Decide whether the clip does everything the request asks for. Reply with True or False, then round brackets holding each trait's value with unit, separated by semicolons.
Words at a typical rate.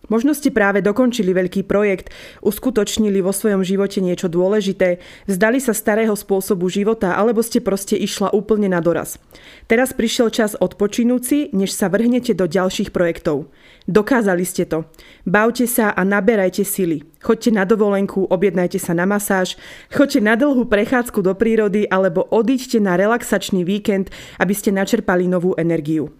True (150 wpm)